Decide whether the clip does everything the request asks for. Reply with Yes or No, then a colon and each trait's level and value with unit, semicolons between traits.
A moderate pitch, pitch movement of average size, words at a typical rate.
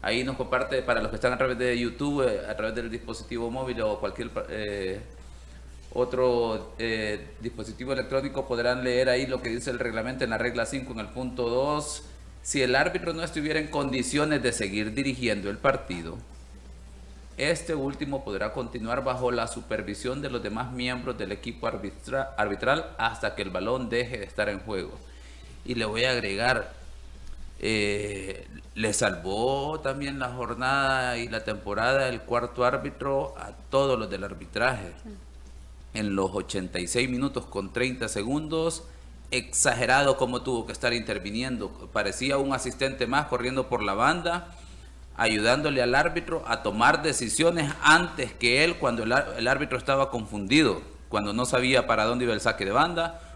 No: low, 125 Hz; average, 4.5 semitones; average, 160 wpm